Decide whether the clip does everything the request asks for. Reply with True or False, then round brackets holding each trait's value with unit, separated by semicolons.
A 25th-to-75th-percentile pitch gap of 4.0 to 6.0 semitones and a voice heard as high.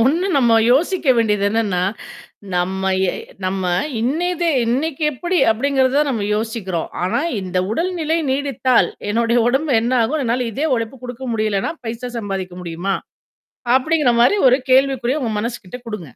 True (4.7 semitones; 240 Hz)